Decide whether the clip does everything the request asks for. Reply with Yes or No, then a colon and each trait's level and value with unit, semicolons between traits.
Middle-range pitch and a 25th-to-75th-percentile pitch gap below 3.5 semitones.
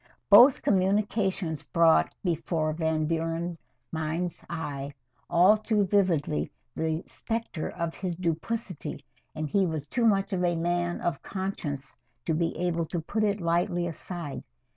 Yes: medium, 170 Hz; average, 3.1 semitones